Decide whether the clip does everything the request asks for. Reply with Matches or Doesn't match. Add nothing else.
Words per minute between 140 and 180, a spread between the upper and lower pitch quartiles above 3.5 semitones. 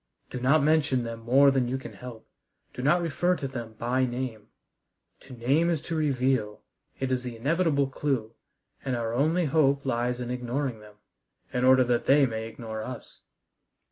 Doesn't match